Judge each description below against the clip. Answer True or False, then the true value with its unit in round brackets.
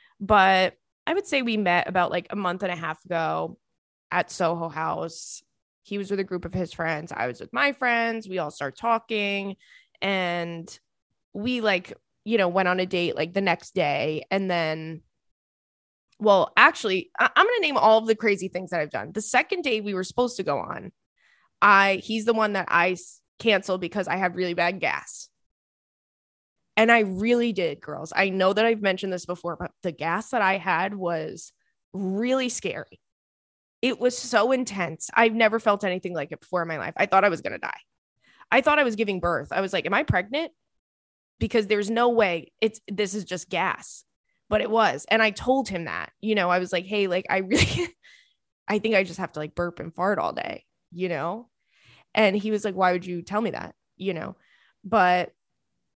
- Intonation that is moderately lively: True (4.0 semitones)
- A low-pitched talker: False (195 Hz)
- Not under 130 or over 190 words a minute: False (205 wpm)